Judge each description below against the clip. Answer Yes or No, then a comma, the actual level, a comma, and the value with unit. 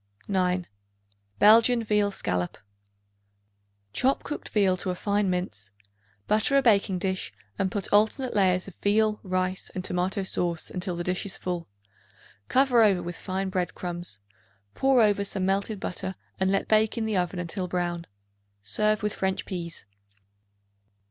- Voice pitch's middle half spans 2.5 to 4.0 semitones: Yes, average, 2.8 semitones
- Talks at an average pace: Yes, average, 150 wpm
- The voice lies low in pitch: No, high, 190 Hz